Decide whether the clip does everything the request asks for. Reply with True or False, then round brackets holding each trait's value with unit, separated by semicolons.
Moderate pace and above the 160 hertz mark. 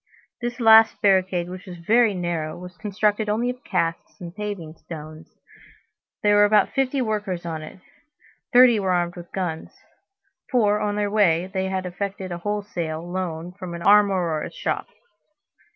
True (155 wpm; 190 Hz)